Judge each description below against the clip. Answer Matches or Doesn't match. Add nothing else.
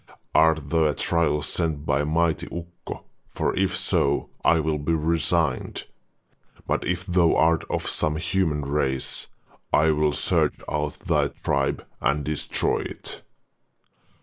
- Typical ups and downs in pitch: Doesn't match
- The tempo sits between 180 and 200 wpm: Doesn't match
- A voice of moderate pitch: Doesn't match